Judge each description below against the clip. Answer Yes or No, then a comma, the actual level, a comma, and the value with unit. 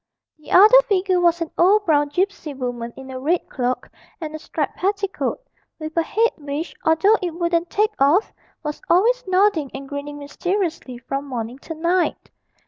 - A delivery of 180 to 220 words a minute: No, average, 170 wpm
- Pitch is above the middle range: Yes, very high, 325 Hz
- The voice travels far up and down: No, average, 4.8 semitones